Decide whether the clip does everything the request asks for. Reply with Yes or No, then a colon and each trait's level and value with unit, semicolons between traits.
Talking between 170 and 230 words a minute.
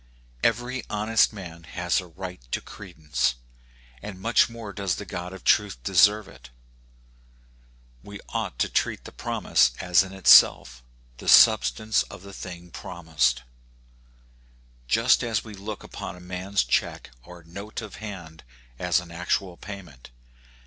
No: average, 145 wpm